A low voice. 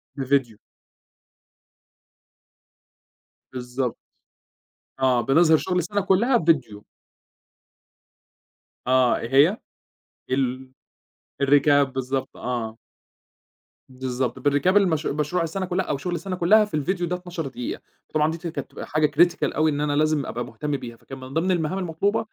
No: medium, 150 Hz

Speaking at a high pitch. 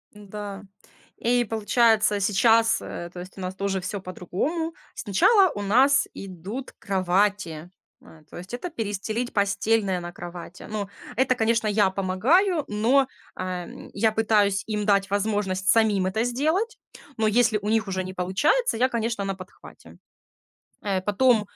Yes: high, 210 Hz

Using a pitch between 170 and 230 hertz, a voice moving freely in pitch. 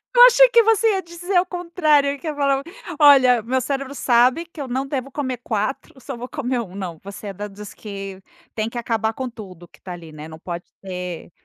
No: very high, 250 Hz; wide, 6.6 semitones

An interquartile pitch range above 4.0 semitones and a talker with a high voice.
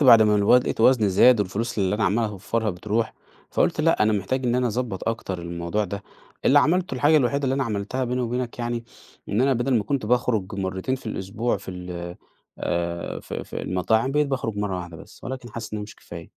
No: average, 4.5 semitones; low, 110 Hz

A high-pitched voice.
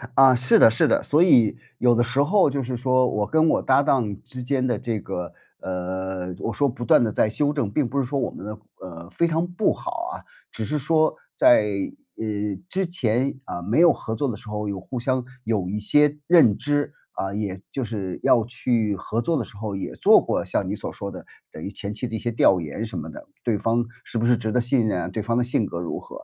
No: low, 120 Hz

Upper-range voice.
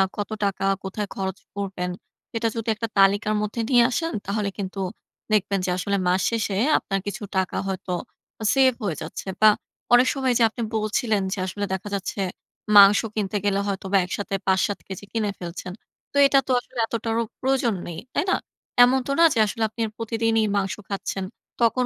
Yes: high, 205 Hz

